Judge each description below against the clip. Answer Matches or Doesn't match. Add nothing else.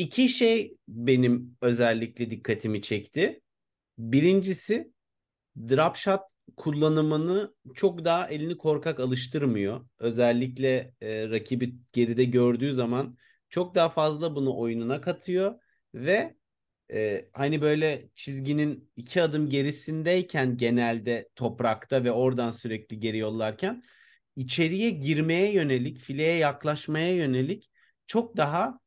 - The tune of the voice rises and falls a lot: Matches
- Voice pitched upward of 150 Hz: Doesn't match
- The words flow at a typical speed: Matches